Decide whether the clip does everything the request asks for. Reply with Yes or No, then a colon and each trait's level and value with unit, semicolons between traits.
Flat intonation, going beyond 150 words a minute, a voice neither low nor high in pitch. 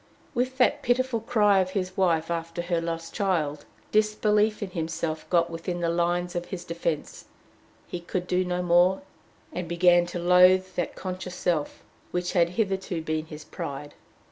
Yes: narrow, 2.1 semitones; average, 165 wpm; medium, 175 Hz